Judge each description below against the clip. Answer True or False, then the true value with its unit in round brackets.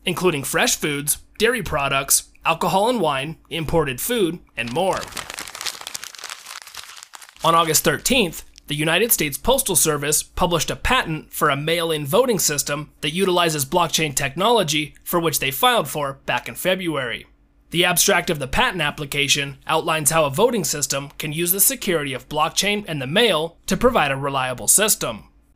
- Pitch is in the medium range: True (160 Hz)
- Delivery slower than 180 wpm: True (155 wpm)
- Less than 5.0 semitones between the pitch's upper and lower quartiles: True (3.8 semitones)